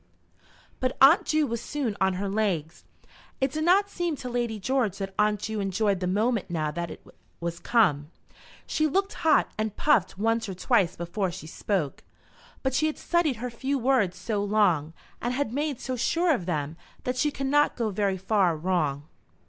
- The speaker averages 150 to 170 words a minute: No, average, 190 wpm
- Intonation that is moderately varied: No, wide, 6.4 semitones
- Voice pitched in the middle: No, high, 215 Hz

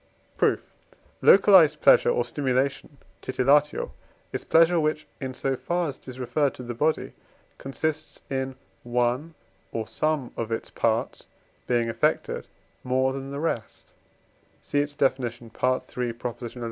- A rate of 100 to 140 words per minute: Yes, slow, 135 wpm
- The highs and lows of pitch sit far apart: No, average, 3.5 semitones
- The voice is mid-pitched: No, low, 130 Hz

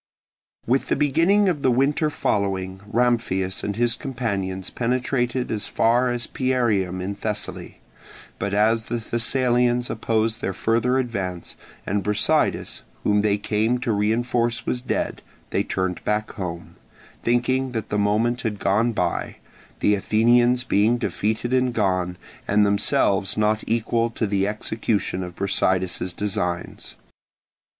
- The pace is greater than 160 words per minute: No, slow, 135 wpm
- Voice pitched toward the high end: No, low, 110 Hz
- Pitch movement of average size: Yes, average, 3.5 semitones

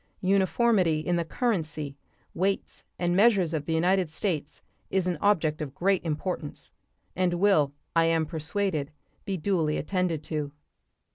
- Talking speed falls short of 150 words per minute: Yes, average, 140 wpm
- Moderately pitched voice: Yes, medium, 175 Hz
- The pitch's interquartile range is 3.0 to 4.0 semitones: Yes, average, 3.7 semitones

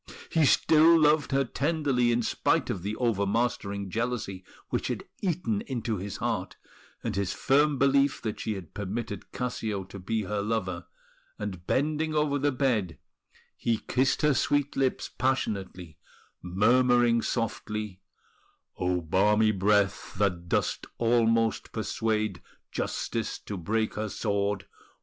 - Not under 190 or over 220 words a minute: No, slow, 135 wpm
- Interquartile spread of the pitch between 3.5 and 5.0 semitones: Yes, average, 4.7 semitones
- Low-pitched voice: Yes, low, 110 Hz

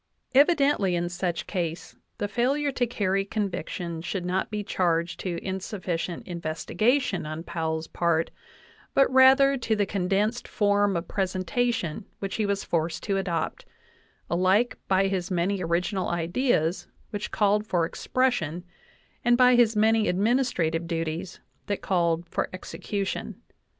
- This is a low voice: No, high, 190 Hz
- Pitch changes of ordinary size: Yes, average, 4.3 semitones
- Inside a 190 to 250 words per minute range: No, slow, 135 wpm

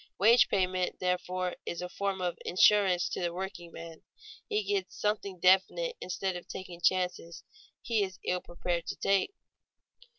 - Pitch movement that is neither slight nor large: No, narrow, 1.9 semitones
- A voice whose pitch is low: No, medium, 185 Hz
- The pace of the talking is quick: No, average, 145 wpm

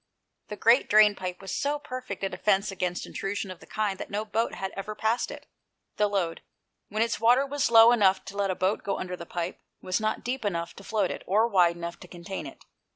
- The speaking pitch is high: Yes, high, 200 Hz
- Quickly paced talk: Yes, fast, 230 wpm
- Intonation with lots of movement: No, average, 3.1 semitones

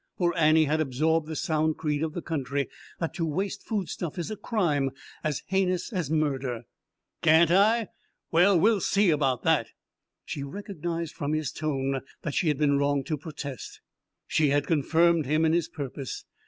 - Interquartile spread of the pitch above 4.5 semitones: No, average, 3.2 semitones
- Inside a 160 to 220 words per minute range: Yes, average, 170 wpm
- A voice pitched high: No, medium, 155 Hz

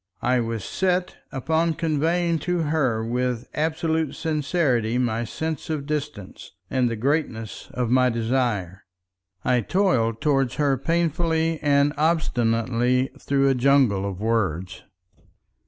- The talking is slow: Yes, slow, 125 wpm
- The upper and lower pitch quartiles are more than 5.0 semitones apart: Yes, wide, 5.5 semitones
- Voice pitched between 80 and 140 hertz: Yes, low, 135 Hz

